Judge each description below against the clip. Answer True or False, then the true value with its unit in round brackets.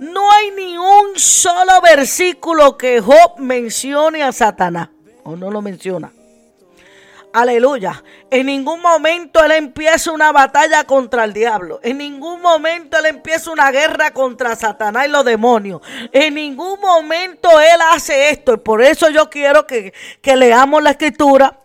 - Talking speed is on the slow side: False (150 wpm)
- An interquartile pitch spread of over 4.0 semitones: True (4.8 semitones)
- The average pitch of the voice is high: True (290 Hz)